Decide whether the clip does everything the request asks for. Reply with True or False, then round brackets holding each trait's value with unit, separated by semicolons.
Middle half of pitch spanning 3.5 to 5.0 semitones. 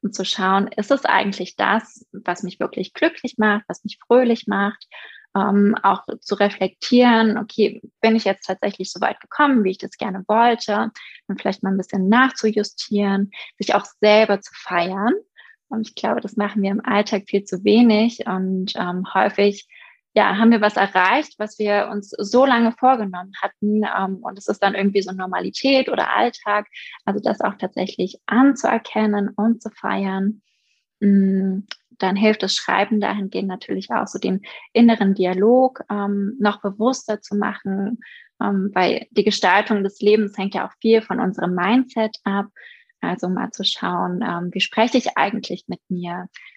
False (2.7 semitones)